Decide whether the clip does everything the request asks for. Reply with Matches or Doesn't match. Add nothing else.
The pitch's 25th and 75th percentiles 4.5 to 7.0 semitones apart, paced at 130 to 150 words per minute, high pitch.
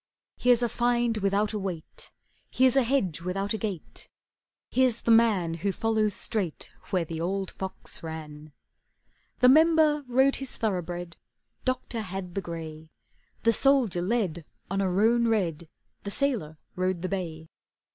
Matches